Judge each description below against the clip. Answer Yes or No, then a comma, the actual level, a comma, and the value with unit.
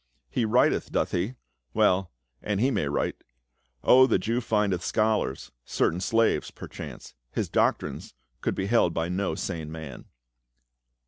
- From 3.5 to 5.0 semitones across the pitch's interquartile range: Yes, average, 4.7 semitones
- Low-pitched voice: Yes, very low, 95 Hz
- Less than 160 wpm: Yes, average, 140 wpm